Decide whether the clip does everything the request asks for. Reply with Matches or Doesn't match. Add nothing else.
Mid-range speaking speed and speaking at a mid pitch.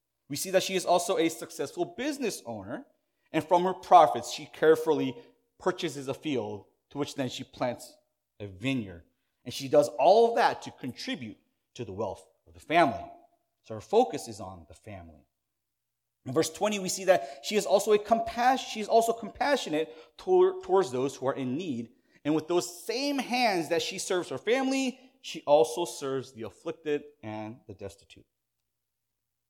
Matches